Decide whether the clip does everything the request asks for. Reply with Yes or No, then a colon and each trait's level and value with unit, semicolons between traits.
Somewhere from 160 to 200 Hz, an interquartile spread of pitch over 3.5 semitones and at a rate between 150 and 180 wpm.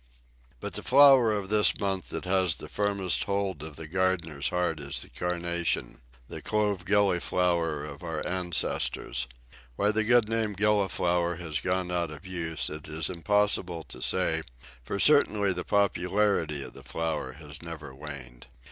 No: very low, 90 Hz; average, 4.1 semitones; average, 160 wpm